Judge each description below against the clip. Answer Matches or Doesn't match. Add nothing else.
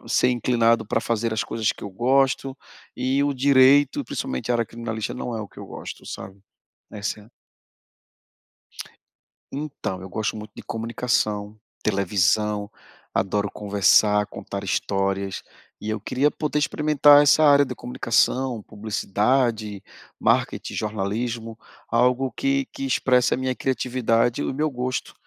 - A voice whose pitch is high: Doesn't match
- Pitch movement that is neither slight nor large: Matches